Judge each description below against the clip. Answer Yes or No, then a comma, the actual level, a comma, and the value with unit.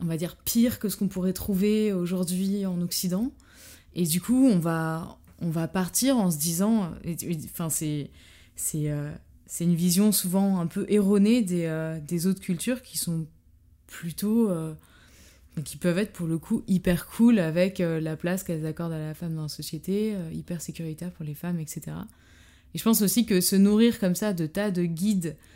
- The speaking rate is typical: Yes, average, 200 wpm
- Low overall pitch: No, medium, 175 Hz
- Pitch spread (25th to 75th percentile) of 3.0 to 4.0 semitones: Yes, average, 3.6 semitones